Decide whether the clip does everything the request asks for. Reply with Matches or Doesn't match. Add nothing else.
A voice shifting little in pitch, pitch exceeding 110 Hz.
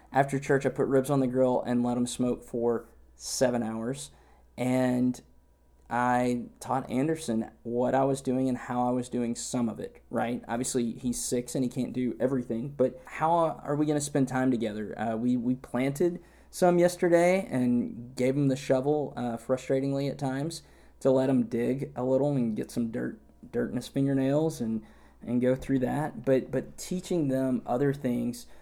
Matches